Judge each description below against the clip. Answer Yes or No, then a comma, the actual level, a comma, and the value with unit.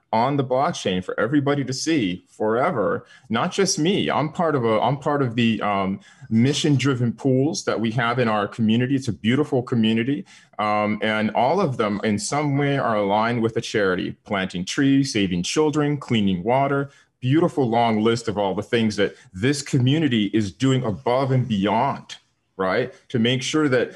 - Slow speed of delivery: No, average, 180 wpm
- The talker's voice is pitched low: Yes, low, 125 Hz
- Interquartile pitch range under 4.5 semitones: No, average, 4.8 semitones